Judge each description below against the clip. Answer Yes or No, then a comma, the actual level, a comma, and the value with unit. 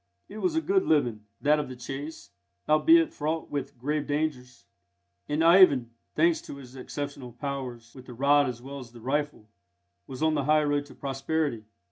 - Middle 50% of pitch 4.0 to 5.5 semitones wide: No, average, 3.3 semitones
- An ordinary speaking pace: Yes, average, 180 wpm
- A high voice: No, medium, 145 Hz